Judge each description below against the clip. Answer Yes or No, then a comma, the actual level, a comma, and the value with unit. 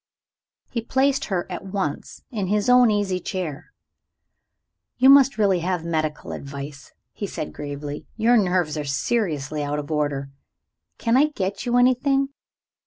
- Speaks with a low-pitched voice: No, medium, 185 Hz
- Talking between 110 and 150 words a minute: Yes, average, 145 wpm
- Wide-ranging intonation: Yes, wide, 8.3 semitones